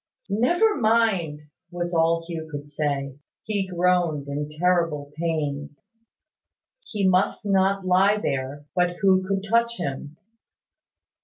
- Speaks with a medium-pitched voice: Yes, medium, 175 Hz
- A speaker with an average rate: No, slow, 120 wpm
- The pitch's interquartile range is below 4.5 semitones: No, average, 4.8 semitones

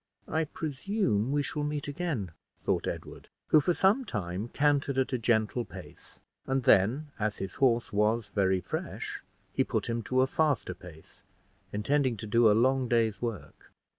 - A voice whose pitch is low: Yes, low, 120 Hz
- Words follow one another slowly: No, average, 165 wpm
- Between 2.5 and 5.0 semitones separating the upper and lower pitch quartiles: No, wide, 5.5 semitones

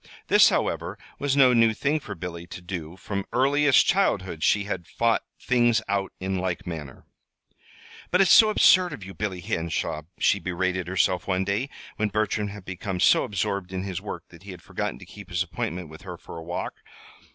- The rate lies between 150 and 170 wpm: No, average, 195 wpm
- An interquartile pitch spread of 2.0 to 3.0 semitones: No, average, 4.0 semitones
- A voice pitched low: Yes, very low, 95 Hz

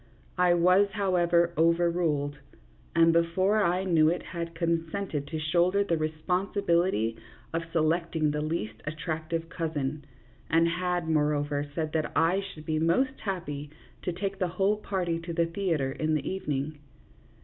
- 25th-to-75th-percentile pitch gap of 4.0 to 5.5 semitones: No, narrow, 2.6 semitones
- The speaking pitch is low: No, medium, 165 Hz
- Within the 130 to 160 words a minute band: Yes, average, 150 wpm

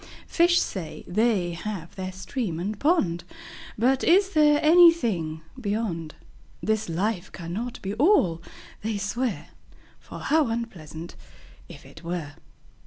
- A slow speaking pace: Yes, slow, 120 wpm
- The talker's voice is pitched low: No, high, 210 Hz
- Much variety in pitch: Yes, wide, 6.9 semitones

